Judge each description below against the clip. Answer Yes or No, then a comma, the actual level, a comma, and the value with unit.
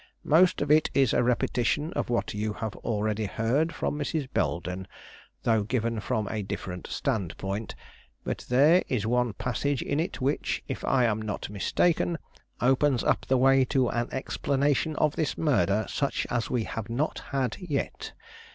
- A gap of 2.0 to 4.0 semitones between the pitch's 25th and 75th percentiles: No, average, 4.9 semitones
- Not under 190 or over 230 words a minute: No, average, 165 wpm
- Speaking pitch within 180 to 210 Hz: No, low, 125 Hz